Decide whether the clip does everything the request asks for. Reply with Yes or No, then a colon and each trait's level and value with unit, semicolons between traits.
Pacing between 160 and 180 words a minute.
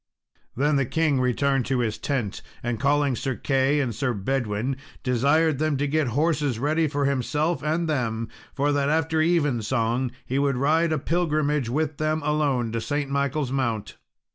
Yes: average, 165 wpm